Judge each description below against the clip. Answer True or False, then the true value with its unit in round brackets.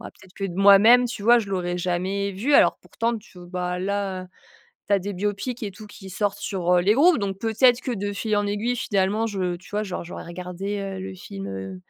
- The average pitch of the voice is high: True (195 Hz)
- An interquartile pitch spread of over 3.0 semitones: False (2.6 semitones)